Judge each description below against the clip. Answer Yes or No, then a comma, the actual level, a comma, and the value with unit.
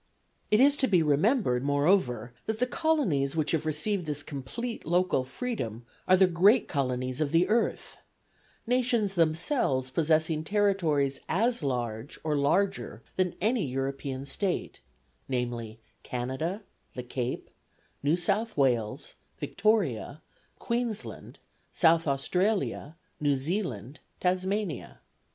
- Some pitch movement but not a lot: No, wide, 7.1 semitones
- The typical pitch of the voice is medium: Yes, medium, 160 Hz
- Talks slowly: Yes, slow, 115 wpm